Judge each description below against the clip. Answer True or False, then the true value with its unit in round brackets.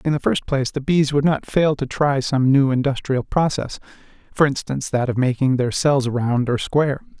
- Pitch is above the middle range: False (135 Hz)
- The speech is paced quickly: True (210 wpm)